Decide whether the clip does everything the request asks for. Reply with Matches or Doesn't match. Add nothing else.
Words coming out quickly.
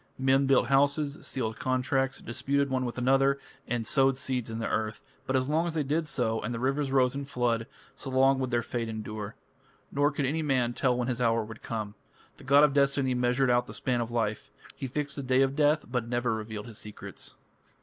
Matches